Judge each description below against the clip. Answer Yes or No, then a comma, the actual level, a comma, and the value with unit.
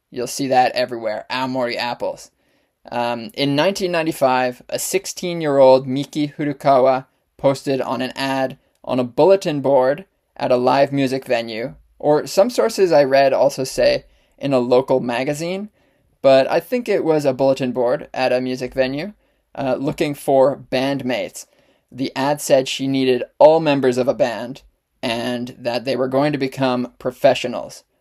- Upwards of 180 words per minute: No, average, 155 wpm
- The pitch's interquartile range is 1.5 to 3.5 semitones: Yes, narrow, 2.5 semitones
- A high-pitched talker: No, low, 135 Hz